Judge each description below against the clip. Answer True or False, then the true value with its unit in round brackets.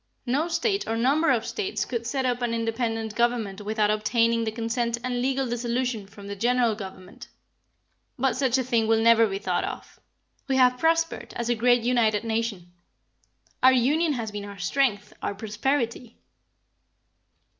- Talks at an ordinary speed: True (165 wpm)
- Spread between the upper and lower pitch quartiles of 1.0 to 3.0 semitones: True (2.6 semitones)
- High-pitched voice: True (235 Hz)